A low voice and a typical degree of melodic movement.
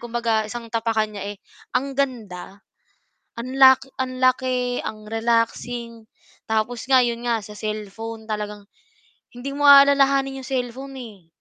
No: high, 235 Hz; average, 3.0 semitones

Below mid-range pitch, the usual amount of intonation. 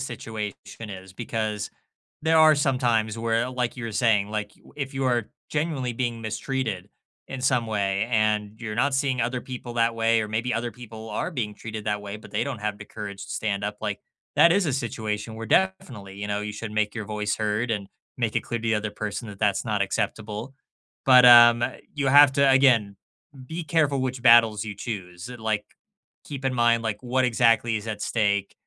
Yes: low, 115 Hz; average, 3.1 semitones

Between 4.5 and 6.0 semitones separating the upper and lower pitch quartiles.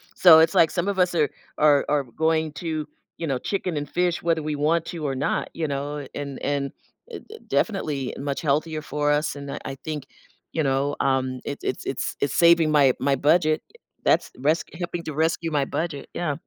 No: average, 2.7 semitones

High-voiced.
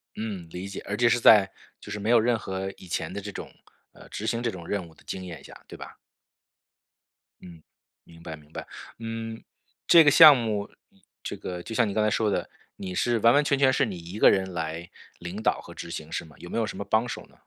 No: low, 100 Hz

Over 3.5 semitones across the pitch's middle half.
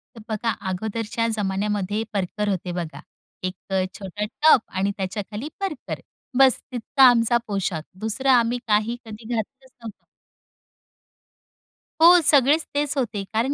Yes: average, 4.0 semitones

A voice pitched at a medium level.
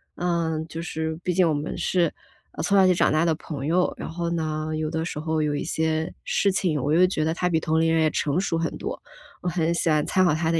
Yes: medium, 160 Hz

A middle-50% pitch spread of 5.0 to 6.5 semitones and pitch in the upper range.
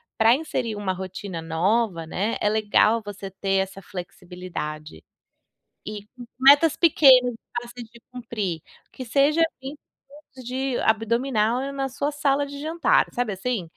Yes: wide, 5.6 semitones; high, 230 Hz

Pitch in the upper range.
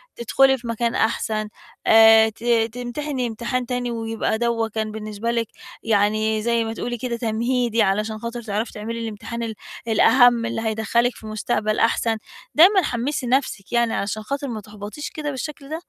Yes: high, 230 Hz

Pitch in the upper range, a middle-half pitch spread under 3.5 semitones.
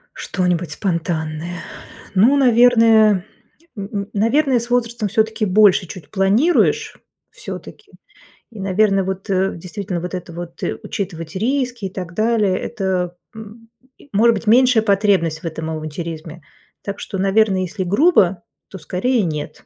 No: high, 195 Hz; average, 4.0 semitones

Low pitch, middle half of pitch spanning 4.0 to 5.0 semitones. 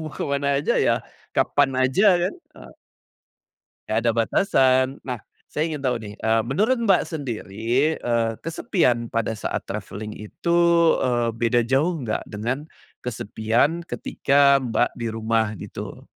Yes: low, 125 Hz; average, 4.6 semitones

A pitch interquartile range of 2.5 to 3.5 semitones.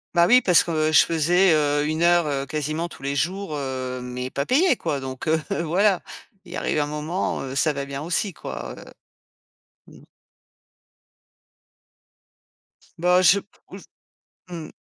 No: average, 3.9 semitones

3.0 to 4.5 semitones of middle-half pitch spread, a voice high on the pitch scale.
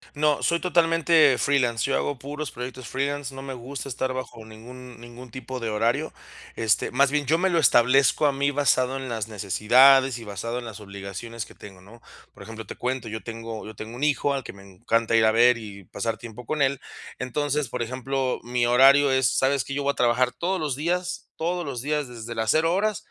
No: average, 3.7 semitones; low, 125 Hz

